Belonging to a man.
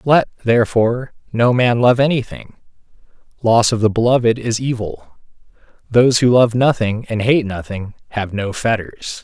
Yes: male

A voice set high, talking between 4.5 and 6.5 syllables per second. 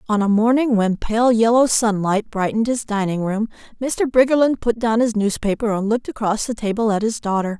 Yes: high, 220 Hz; 5.5 syllables/s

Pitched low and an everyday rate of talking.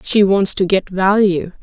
No: high, 190 Hz; average, 185 wpm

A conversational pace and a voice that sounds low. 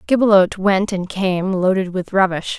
No: average, 160 wpm; high, 190 Hz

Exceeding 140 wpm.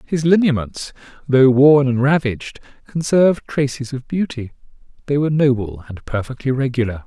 No: slow, 135 wpm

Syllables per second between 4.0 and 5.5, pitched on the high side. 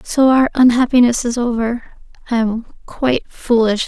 Yes: 4.7 syllables/s; high, 240 Hz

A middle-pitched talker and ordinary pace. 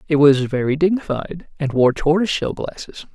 Yes: medium, 150 Hz; average, 170 wpm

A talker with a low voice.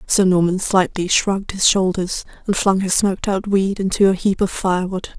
No: high, 190 Hz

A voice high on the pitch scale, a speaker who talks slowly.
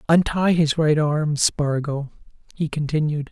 No: medium, 150 Hz; slow, 125 wpm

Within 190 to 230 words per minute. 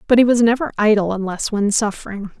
Yes: average, 200 wpm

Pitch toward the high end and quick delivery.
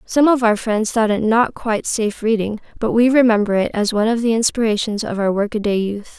Yes: high, 220 Hz; fast, 225 wpm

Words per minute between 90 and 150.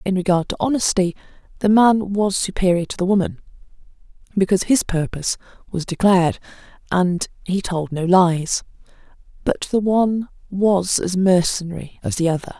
Yes: average, 140 wpm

